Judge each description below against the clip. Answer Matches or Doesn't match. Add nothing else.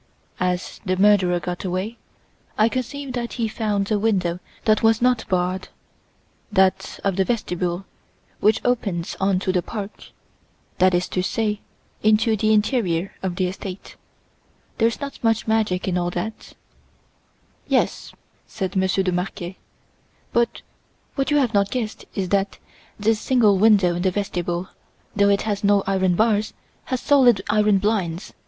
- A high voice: Matches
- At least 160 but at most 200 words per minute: Doesn't match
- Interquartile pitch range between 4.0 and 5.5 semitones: Doesn't match